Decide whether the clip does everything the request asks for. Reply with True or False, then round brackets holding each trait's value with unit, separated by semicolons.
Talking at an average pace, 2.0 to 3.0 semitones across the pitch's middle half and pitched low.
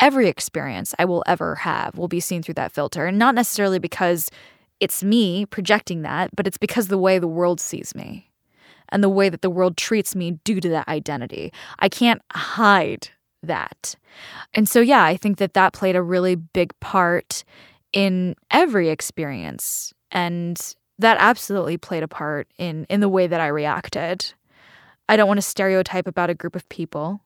False (185 wpm; 2.7 semitones; 185 Hz)